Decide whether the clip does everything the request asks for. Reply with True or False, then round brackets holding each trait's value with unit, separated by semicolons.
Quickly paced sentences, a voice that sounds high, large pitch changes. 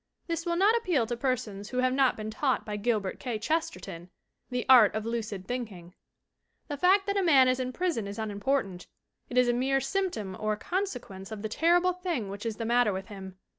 True (210 wpm; 245 Hz; 5.9 semitones)